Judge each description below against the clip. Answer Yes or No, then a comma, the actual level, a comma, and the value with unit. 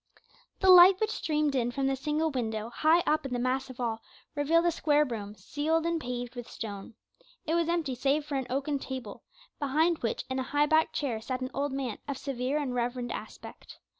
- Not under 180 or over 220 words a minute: Yes, fast, 205 wpm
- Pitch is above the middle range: Yes, very high, 275 Hz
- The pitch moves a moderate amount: Yes, average, 3.9 semitones